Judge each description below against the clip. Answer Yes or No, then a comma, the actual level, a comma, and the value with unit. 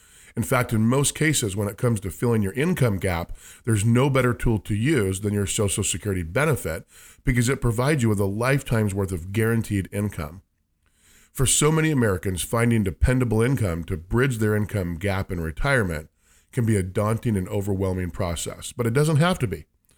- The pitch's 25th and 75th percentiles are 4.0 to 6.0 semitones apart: Yes, average, 4.4 semitones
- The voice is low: Yes, low, 105 Hz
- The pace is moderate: Yes, average, 185 wpm